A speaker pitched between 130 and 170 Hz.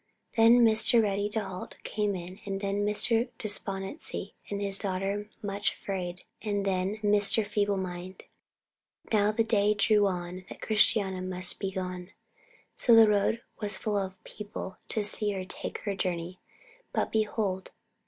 No: high, 200 Hz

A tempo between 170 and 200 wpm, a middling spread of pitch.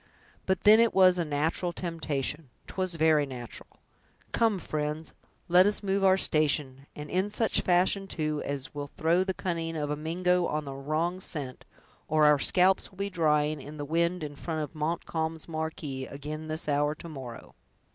Yes: average, 175 wpm; average, 3.3 semitones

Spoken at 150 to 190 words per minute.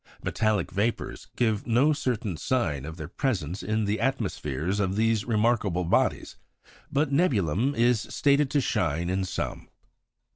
No: average, 140 wpm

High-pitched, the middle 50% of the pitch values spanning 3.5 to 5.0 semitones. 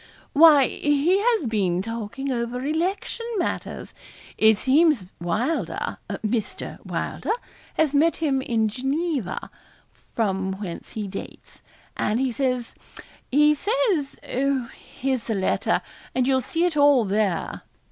No: very high, 260 Hz; wide, 5.5 semitones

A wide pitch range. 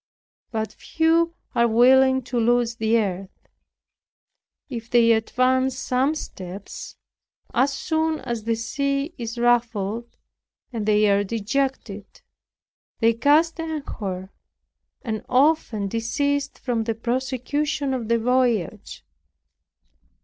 No: average, 3.7 semitones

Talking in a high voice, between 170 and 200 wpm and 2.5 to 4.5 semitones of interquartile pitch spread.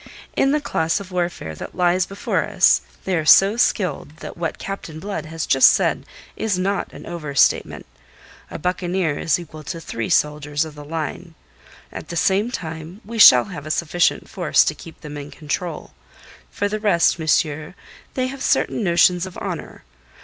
No: medium, 170 Hz; average, 175 wpm; average, 3.7 semitones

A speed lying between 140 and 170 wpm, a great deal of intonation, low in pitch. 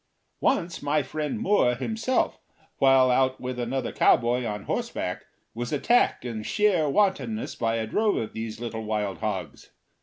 Yes: average, 150 wpm; wide, 6.6 semitones; low, 125 Hz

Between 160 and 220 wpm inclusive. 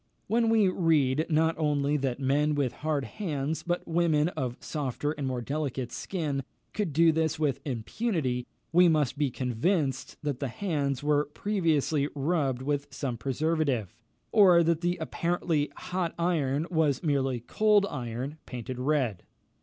No: average, 145 wpm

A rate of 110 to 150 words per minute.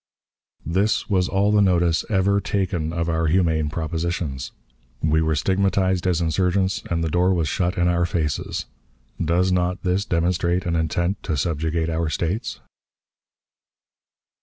Yes: average, 140 wpm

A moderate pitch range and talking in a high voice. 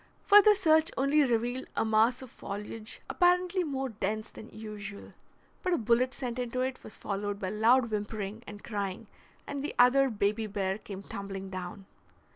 Yes: average, 4.4 semitones; high, 225 Hz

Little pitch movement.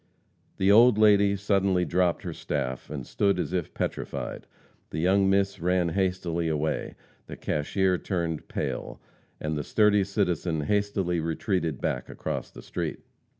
No: average, 3.2 semitones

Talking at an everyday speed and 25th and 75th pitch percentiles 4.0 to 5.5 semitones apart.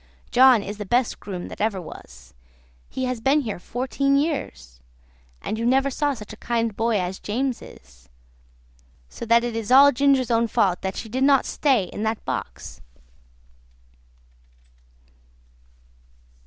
Yes: average, 150 wpm; average, 4.4 semitones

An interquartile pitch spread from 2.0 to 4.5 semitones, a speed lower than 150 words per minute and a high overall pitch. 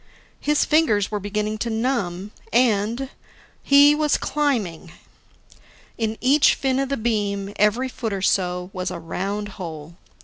No: average, 5.1 semitones; average, 140 wpm; high, 210 Hz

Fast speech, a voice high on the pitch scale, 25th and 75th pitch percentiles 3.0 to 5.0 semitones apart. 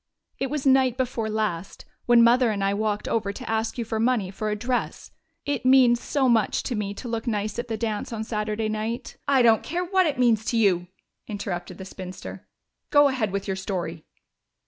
Yes: fast, 210 wpm; high, 220 Hz; average, 3.4 semitones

